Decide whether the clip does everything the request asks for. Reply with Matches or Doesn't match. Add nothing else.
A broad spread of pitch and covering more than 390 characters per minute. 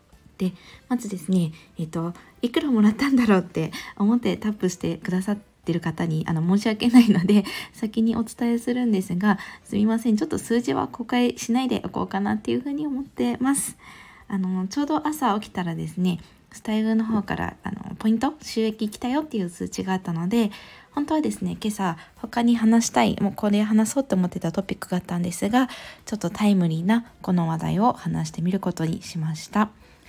Doesn't match